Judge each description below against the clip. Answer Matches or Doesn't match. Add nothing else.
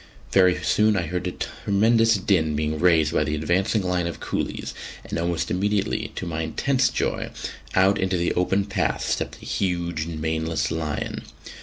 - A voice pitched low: Matches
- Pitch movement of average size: Matches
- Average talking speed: Matches